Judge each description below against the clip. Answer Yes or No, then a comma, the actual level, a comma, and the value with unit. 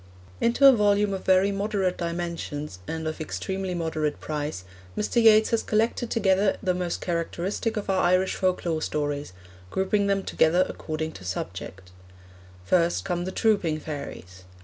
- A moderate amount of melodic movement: Yes, average, 4.2 semitones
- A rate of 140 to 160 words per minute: Yes, average, 150 wpm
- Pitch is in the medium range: Yes, medium, 180 Hz